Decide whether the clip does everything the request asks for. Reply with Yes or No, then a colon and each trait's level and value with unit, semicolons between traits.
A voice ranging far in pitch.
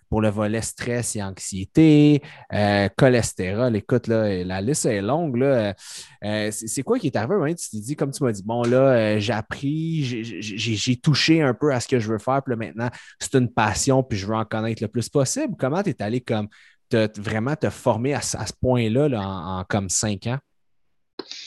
No: average, 4.4 semitones